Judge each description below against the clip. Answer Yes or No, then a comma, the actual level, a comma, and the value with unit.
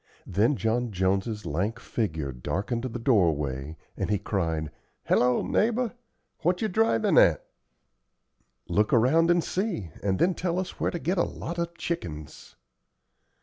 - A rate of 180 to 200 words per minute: No, average, 145 wpm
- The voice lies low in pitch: Yes, low, 115 Hz